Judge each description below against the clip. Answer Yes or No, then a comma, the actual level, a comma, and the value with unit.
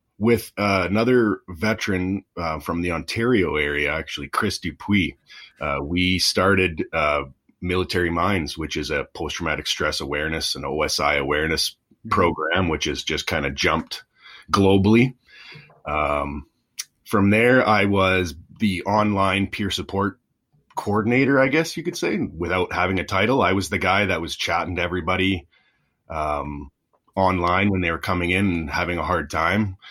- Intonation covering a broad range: No, average, 3.1 semitones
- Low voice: Yes, very low, 95 Hz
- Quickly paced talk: No, average, 150 wpm